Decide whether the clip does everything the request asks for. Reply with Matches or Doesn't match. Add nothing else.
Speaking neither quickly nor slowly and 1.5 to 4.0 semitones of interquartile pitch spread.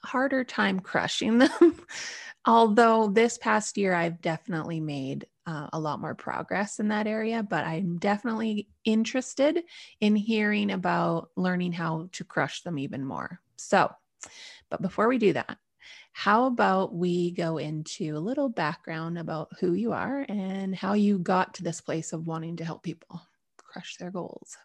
Doesn't match